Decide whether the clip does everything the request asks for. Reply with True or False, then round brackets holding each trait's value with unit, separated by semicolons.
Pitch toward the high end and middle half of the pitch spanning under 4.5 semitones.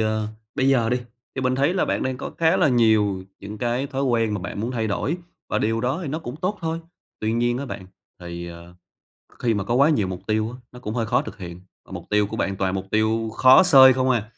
False (115 Hz; 4.0 semitones)